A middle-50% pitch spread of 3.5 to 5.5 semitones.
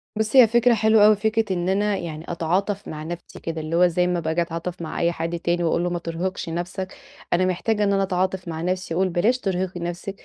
No: average, 2.8 semitones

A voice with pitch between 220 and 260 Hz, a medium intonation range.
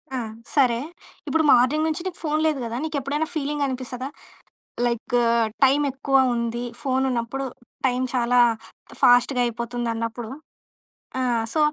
Yes: very high, 255 Hz; average, 3.0 semitones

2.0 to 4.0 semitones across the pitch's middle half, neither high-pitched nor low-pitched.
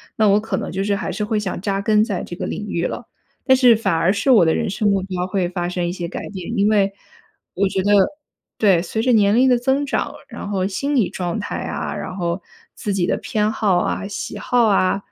No: average, 2.8 semitones; high, 200 Hz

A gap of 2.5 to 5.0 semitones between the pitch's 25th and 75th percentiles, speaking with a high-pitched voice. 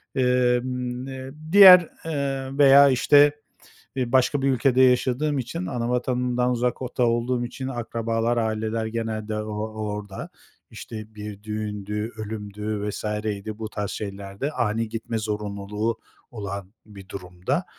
No: average, 3.2 semitones; low, 115 Hz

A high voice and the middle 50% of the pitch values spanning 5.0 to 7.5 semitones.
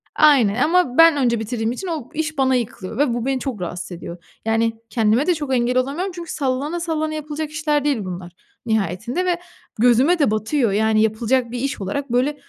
Yes: very high, 255 Hz; average, 5.3 semitones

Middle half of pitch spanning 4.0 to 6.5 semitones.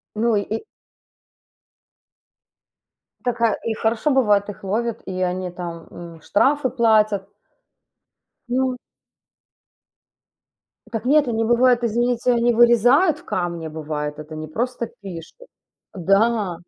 Yes: average, 4.8 semitones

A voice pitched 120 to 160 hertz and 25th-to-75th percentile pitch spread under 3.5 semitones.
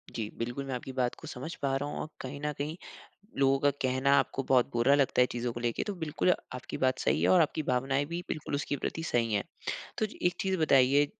Yes: low, 135 Hz; average, 2.7 semitones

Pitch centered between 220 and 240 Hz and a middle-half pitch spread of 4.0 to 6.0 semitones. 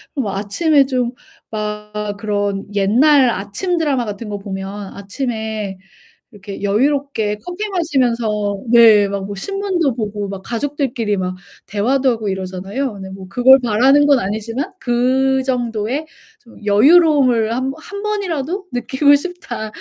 Yes: high, 235 Hz; average, 5.3 semitones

